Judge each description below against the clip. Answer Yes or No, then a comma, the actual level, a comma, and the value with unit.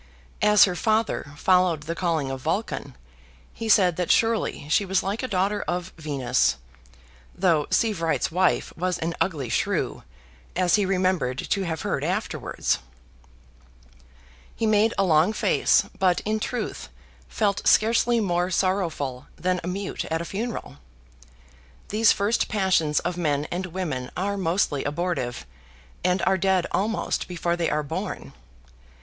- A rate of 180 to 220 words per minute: No, average, 145 wpm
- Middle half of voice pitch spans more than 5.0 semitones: No, average, 3.8 semitones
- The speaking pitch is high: No, medium, 180 Hz